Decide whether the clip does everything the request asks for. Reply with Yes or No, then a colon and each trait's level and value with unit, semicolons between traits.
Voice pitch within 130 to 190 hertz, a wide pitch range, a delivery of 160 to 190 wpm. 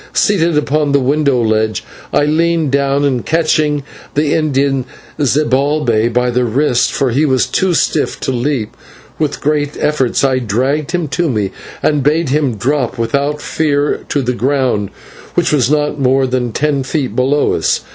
No: medium, 140 Hz; average, 3.1 semitones; average, 165 wpm